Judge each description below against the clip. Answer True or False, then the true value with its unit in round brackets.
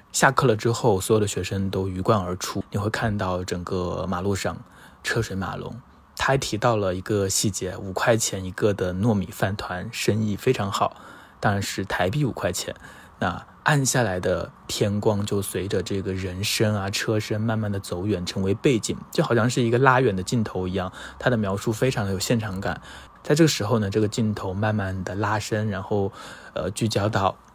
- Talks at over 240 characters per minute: True (285 characters per minute)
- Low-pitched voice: True (105 Hz)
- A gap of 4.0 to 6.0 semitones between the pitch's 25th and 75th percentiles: False (3.0 semitones)